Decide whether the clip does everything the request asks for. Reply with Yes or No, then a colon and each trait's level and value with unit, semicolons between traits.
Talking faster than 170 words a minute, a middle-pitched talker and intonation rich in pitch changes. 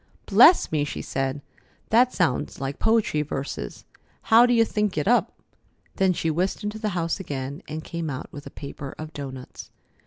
Yes: average, 180 wpm; medium, 165 Hz; wide, 6.8 semitones